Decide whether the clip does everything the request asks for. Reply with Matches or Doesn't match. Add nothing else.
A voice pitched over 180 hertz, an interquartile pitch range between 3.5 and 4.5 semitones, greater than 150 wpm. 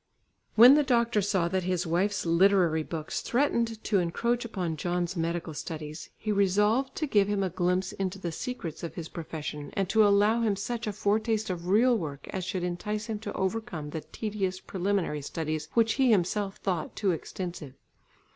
Matches